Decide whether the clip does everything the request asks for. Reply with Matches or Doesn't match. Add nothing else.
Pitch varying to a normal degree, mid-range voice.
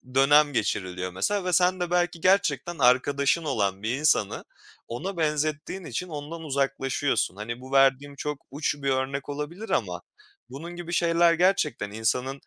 Matches